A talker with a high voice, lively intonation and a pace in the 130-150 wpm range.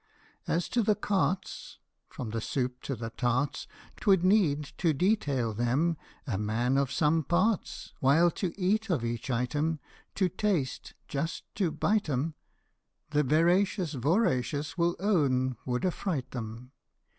No: medium, 150 Hz; wide, 6.3 semitones; average, 145 wpm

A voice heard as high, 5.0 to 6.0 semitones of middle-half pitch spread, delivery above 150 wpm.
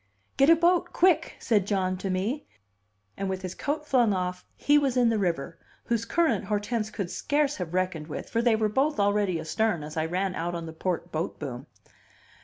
Yes: high, 200 Hz; wide, 5.6 semitones; fast, 205 wpm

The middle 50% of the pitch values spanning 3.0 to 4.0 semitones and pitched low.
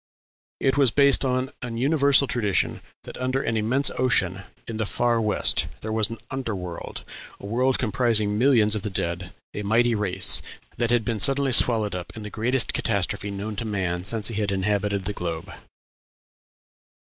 Yes: average, 3.6 semitones; low, 110 Hz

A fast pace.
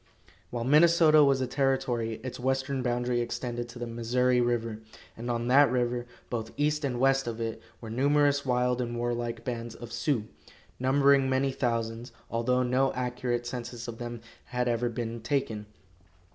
No: average, 160 wpm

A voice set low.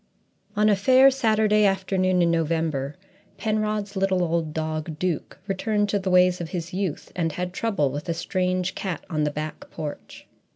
No: medium, 180 Hz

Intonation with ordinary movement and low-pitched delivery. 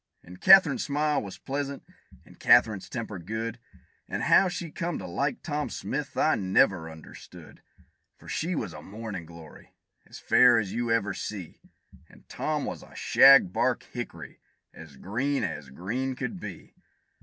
No: wide, 7.5 semitones; low, 115 Hz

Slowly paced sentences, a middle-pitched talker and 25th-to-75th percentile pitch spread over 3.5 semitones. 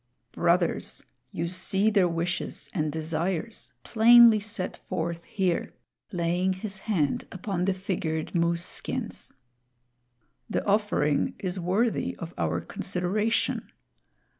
No: slow, 110 wpm; medium, 180 Hz; average, 3.2 semitones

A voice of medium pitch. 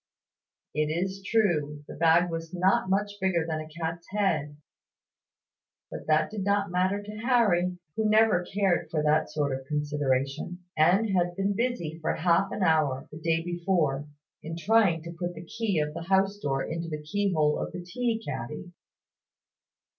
Yes: medium, 175 Hz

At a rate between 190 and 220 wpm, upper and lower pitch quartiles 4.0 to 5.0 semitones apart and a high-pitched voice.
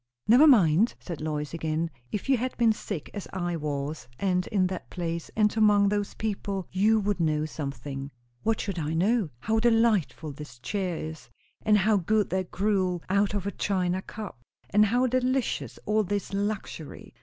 No: average, 175 wpm; average, 4.6 semitones; high, 195 Hz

